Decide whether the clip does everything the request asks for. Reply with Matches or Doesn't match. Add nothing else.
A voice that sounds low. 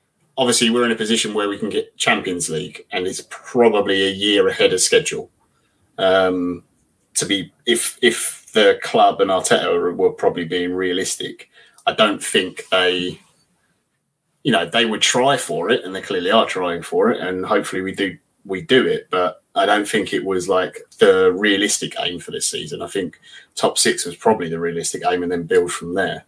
Matches